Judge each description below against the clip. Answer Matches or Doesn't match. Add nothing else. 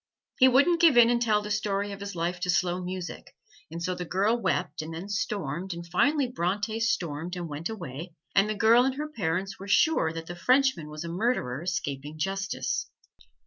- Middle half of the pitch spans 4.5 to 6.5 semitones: Matches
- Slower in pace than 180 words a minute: Doesn't match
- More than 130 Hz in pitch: Matches